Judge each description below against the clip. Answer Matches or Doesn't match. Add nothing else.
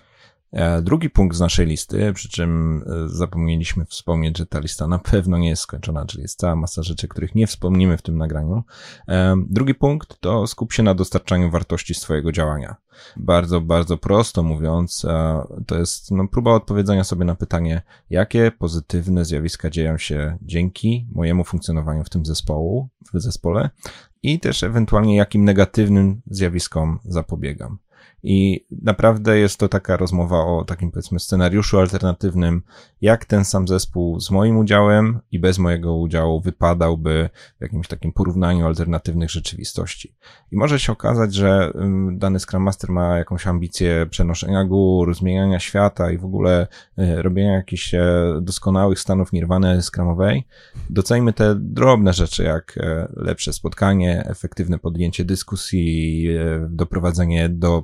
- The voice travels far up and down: Doesn't match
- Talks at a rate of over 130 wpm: Matches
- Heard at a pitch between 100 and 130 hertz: Doesn't match